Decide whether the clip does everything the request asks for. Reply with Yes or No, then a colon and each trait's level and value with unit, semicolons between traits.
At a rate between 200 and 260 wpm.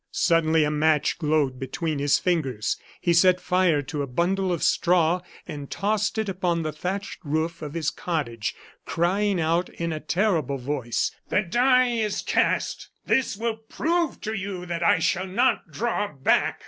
No: average, 165 wpm